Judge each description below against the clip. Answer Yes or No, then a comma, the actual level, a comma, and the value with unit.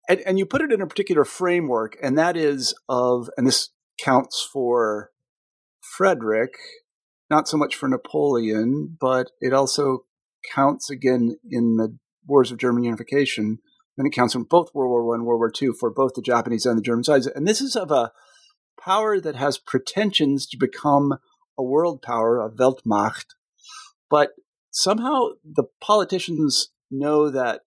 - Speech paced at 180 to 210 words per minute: No, average, 165 wpm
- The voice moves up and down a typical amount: No, wide, 7.7 semitones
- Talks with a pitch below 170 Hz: Yes, medium, 140 Hz